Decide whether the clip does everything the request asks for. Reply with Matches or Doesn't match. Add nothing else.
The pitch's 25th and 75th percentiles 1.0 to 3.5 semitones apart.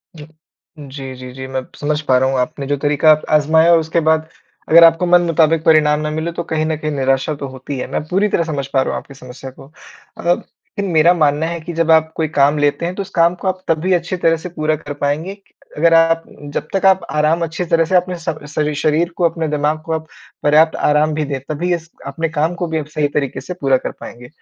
Matches